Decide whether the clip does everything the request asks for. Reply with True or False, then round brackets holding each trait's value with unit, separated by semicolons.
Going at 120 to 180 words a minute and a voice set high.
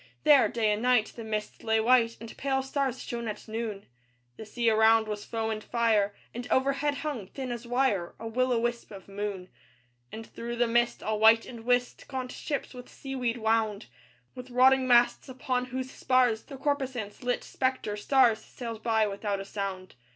False (190 wpm; 235 Hz)